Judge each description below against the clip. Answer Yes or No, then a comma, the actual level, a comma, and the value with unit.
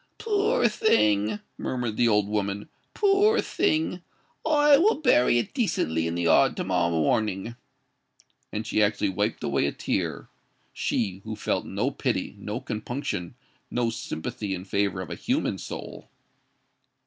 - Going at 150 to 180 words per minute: No, average, 140 wpm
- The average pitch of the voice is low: Yes, low, 105 Hz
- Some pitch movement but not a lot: No, wide, 8.5 semitones